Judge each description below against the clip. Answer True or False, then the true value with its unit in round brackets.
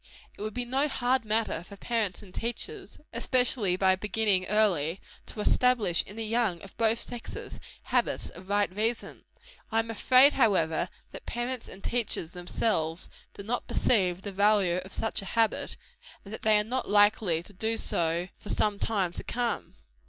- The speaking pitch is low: False (210 Hz)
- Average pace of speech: True (175 wpm)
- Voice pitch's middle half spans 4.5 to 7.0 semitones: False (3.7 semitones)